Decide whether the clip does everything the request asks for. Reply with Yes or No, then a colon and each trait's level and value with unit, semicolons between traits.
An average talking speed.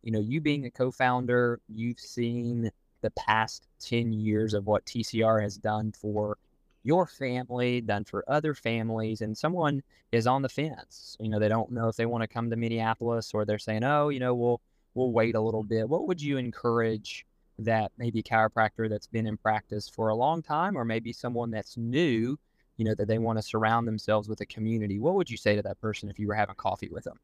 No: fast, 220 wpm